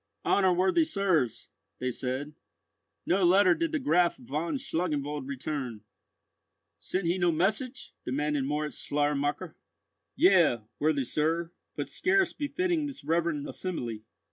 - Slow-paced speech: Yes, slow, 120 wpm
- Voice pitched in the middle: Yes, medium, 165 Hz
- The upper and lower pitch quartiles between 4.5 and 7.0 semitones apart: Yes, average, 5.1 semitones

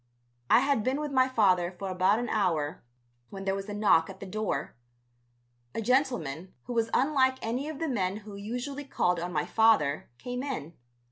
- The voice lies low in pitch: No, high, 215 Hz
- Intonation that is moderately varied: No, wide, 5.9 semitones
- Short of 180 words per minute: No, average, 190 wpm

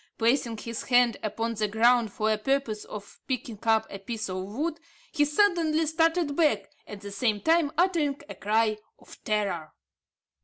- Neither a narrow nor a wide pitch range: No, wide, 5.7 semitones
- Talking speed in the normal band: Yes, average, 165 wpm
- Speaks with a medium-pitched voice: No, high, 230 Hz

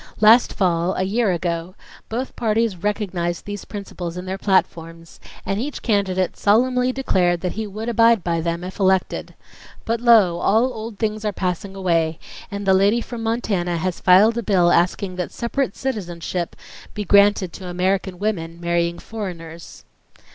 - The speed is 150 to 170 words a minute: Yes, average, 160 wpm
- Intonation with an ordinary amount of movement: Yes, average, 3.9 semitones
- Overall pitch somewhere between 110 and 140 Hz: No, high, 190 Hz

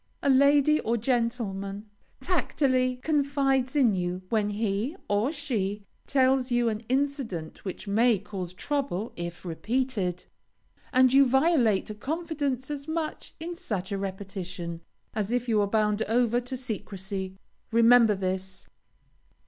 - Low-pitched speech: No, high, 230 Hz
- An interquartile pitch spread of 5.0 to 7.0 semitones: Yes, average, 5.3 semitones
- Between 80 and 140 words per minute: Yes, slow, 135 wpm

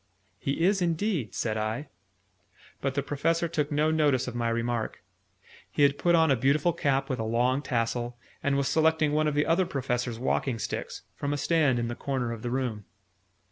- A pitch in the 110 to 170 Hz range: Yes, medium, 140 Hz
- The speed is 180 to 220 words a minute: Yes, average, 195 wpm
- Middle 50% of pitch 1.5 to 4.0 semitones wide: No, average, 4.4 semitones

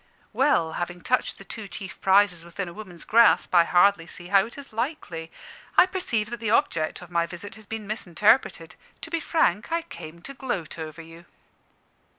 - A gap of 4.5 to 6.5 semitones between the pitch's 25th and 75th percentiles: Yes, average, 5.3 semitones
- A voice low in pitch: No, high, 195 Hz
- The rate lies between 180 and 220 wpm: Yes, average, 185 wpm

